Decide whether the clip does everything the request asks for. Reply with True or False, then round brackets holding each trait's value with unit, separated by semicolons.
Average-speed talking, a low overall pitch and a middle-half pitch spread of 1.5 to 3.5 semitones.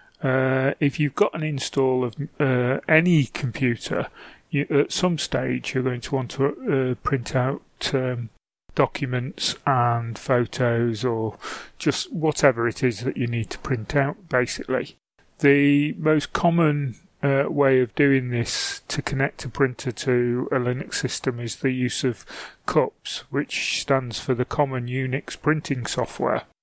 True (150 wpm; 130 Hz; 2.5 semitones)